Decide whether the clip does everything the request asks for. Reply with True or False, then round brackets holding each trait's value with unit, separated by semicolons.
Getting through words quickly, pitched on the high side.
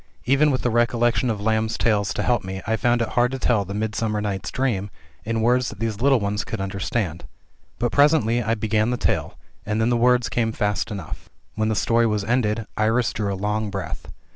False (215 wpm; 110 Hz)